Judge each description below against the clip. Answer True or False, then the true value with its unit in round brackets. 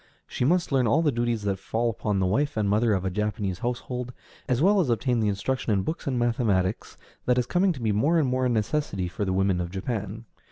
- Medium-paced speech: False (240 wpm)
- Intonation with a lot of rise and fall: False (4.2 semitones)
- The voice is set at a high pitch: False (115 Hz)